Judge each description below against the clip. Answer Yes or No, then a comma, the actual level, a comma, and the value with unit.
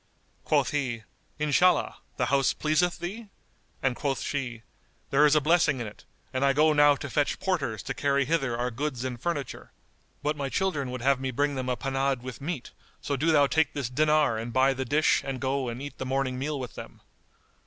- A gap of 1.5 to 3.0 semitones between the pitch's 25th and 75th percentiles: Yes, average, 2.7 semitones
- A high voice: No, medium, 140 Hz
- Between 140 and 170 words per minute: No, fast, 205 wpm